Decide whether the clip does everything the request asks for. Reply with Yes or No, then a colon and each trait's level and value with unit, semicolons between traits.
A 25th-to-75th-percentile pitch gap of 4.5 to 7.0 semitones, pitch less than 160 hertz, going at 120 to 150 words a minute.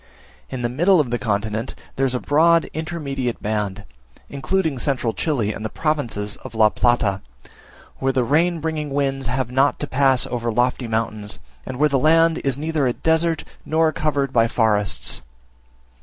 No: average, 5.0 semitones; low, 135 Hz; average, 170 wpm